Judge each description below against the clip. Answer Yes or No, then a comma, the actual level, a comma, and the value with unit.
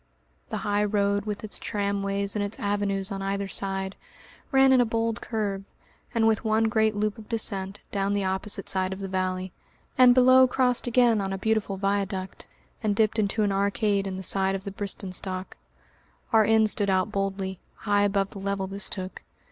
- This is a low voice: No, high, 200 Hz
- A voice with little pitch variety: Yes, narrow, 2.0 semitones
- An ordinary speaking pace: Yes, average, 190 wpm